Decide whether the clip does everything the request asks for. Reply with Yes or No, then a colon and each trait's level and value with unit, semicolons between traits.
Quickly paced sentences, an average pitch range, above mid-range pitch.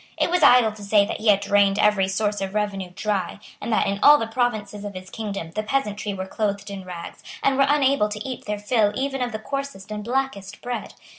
Yes: fast, 230 wpm; average, 3.5 semitones; high, 210 Hz